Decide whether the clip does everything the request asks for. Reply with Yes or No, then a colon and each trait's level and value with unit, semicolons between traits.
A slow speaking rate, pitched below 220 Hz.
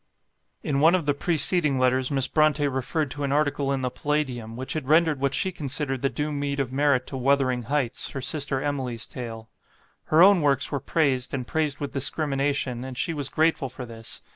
No: average, 200 wpm; medium, 140 Hz